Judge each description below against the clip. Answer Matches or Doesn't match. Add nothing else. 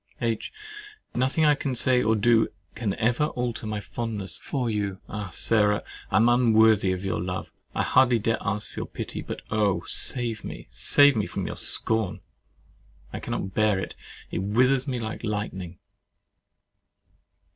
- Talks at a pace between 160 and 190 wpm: Doesn't match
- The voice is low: Matches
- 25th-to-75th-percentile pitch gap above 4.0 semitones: Doesn't match